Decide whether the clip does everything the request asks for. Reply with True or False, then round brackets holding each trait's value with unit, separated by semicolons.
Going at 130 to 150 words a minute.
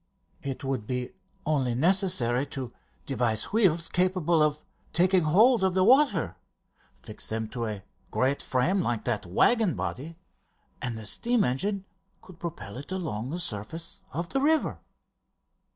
True (145 wpm)